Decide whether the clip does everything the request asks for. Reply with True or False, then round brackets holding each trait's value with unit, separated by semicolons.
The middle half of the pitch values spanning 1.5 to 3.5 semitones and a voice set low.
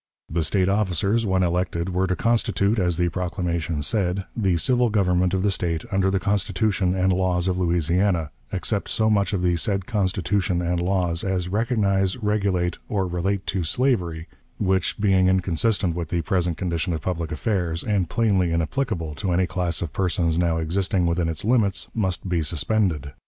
True (2.5 semitones; 90 Hz)